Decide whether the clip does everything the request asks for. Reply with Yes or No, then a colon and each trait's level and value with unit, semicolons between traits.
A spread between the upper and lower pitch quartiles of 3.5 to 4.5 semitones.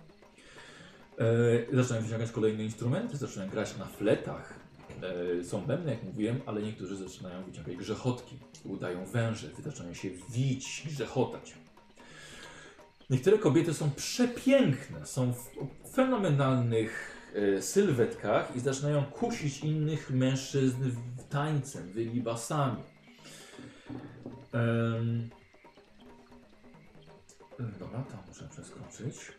Yes: average, 3.8 semitones